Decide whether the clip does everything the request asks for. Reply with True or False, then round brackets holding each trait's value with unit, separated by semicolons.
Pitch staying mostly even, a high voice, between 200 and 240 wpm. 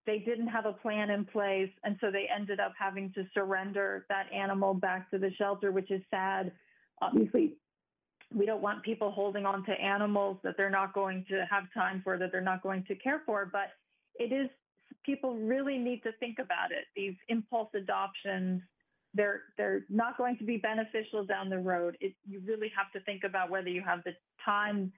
True (2.3 semitones; 200 Hz; 205 wpm)